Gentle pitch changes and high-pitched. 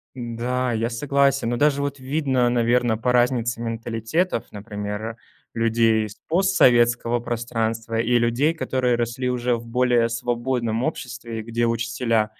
No: narrow, 1.7 semitones; low, 120 Hz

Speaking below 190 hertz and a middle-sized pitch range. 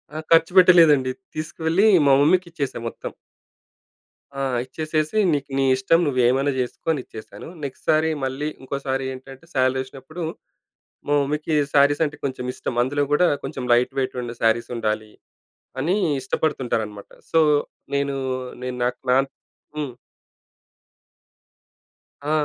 Yes: low, 135 Hz; average, 3.3 semitones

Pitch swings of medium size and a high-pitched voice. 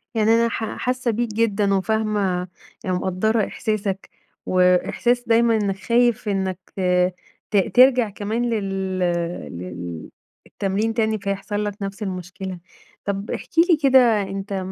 Yes: average, 3.1 semitones; high, 205 Hz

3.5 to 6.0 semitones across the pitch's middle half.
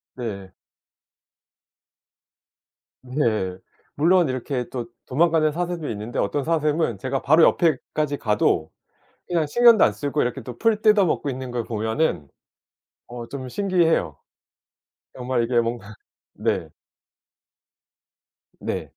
Yes: wide, 5.6 semitones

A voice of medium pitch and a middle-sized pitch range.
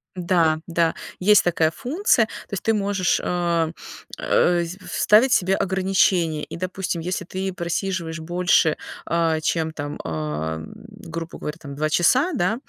Yes: medium, 175 Hz; average, 3.0 semitones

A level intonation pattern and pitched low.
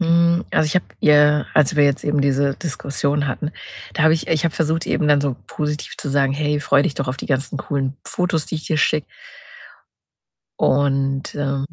No: narrow, 2.0 semitones; medium, 145 Hz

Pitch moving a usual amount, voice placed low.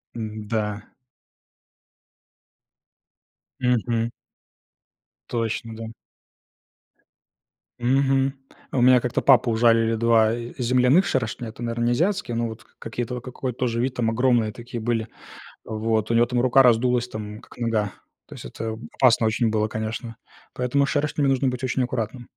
No: narrow, 2.1 semitones; low, 120 Hz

